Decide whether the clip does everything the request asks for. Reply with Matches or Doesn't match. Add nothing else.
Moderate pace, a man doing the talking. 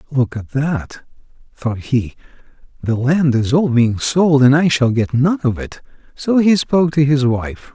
Matches